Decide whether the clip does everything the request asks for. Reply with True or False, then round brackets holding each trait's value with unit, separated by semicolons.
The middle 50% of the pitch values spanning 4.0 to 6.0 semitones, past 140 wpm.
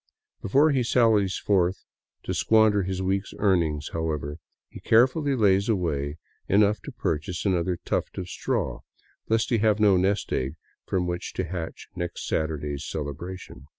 True (4.6 semitones; 150 wpm)